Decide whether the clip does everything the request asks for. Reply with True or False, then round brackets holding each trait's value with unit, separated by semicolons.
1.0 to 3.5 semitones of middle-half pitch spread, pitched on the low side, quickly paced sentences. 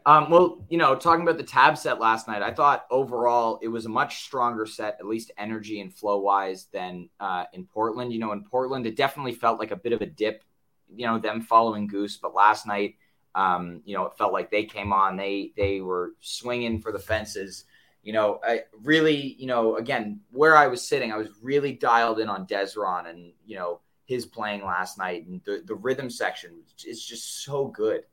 False (4.2 semitones; 110 Hz; 215 wpm)